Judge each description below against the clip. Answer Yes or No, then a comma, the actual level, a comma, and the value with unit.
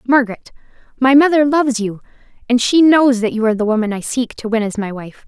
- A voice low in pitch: No, high, 240 Hz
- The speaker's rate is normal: No, fast, 225 wpm